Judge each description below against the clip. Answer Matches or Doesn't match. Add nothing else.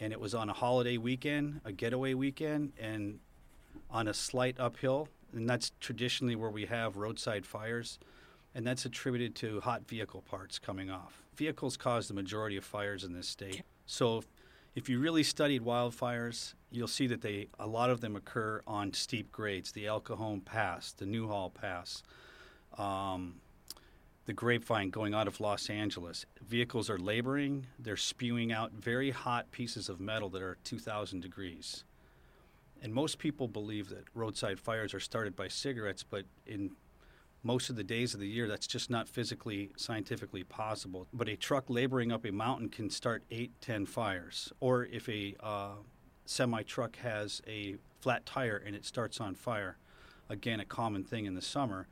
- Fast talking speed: Doesn't match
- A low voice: Matches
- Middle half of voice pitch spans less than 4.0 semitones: Matches